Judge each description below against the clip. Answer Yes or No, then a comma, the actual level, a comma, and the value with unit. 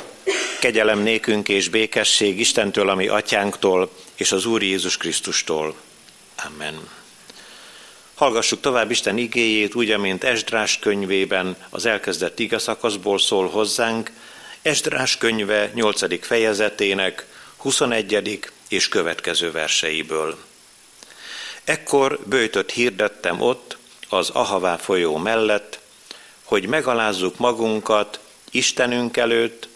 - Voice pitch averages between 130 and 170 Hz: No, low, 110 Hz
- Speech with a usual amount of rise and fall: Yes, average, 3.0 semitones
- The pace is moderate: No, slow, 95 wpm